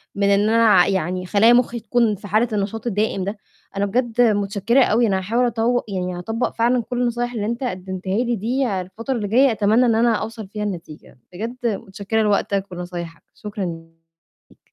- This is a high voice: Yes, high, 215 Hz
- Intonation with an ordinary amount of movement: Yes, average, 3.3 semitones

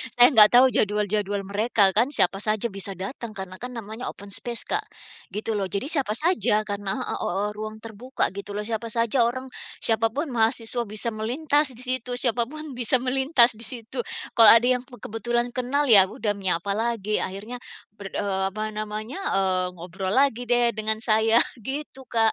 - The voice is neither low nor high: No, high, 225 Hz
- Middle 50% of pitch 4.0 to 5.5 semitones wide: No, average, 3.3 semitones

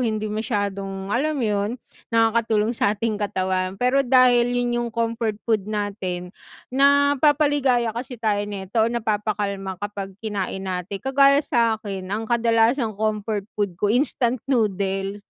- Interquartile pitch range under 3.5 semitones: Yes, average, 3.1 semitones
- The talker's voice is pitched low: No, high, 220 Hz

